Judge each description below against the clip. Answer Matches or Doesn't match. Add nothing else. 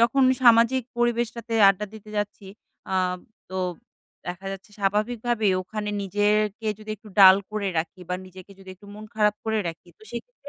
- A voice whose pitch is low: Doesn't match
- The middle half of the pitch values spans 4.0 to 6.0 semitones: Doesn't match